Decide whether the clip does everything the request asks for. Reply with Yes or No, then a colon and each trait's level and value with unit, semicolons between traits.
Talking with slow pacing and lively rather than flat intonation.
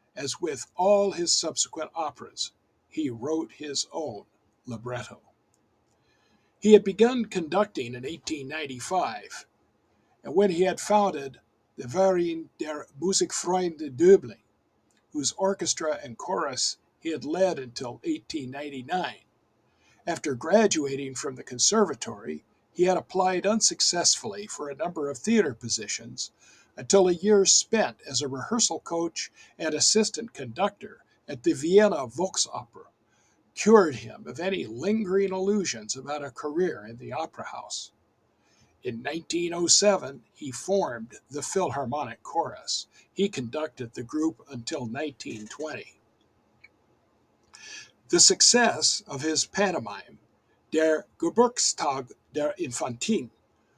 Yes: slow, 115 wpm; wide, 6.4 semitones